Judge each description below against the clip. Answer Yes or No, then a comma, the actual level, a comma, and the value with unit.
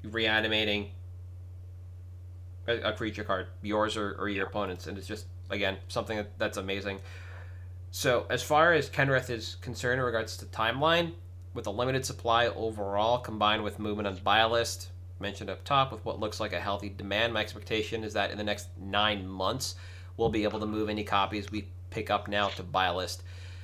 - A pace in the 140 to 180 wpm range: No, average, 190 wpm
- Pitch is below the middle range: Yes, low, 100 Hz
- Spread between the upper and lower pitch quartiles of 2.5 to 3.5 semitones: Yes, average, 3.0 semitones